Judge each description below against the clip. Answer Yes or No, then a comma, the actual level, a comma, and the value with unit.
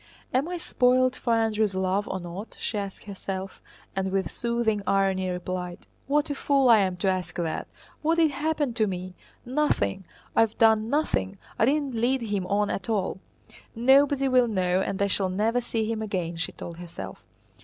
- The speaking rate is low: No, average, 185 wpm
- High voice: Yes, high, 210 Hz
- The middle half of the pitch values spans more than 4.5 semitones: Yes, average, 5.0 semitones